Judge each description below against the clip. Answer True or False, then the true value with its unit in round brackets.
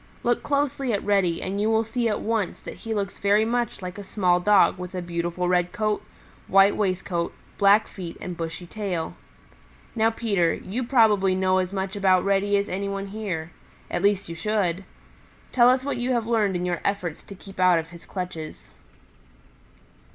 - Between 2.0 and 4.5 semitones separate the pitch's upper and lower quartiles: True (3.2 semitones)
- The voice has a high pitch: True (195 Hz)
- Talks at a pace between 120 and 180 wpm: False (190 wpm)